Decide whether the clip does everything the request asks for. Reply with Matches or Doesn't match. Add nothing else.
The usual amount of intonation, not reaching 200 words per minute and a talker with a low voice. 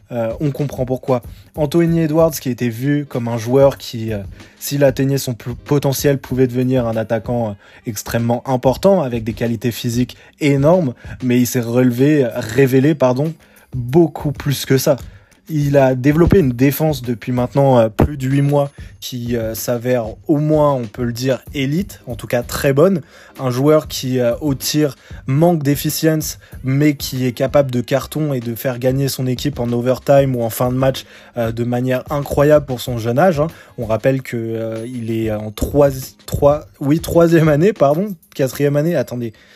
Matches